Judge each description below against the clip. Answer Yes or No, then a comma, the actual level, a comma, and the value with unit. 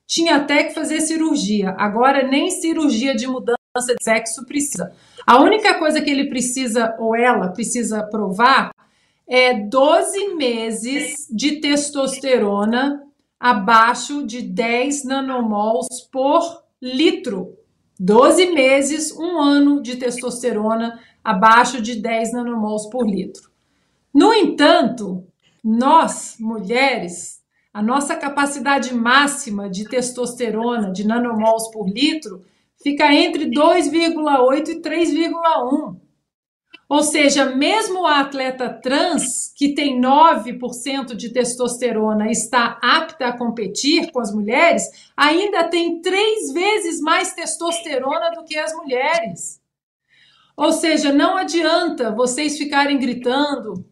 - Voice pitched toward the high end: Yes, very high, 270 Hz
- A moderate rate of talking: No, slow, 110 wpm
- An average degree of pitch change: Yes, average, 4.6 semitones